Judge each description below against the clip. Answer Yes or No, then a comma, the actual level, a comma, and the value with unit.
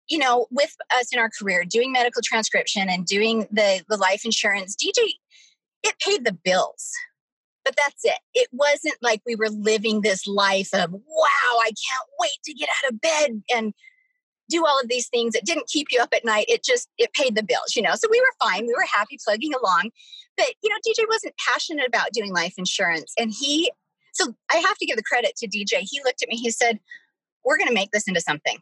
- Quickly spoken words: Yes, fast, 220 wpm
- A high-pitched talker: Yes, high, 240 Hz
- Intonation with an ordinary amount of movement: No, wide, 6.9 semitones